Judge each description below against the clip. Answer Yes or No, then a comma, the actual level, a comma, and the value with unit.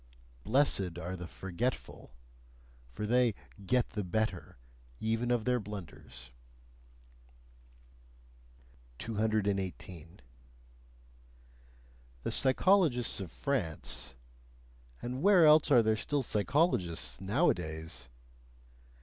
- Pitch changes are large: Yes, wide, 5.8 semitones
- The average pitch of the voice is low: Yes, low, 110 Hz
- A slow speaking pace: Yes, slow, 80 wpm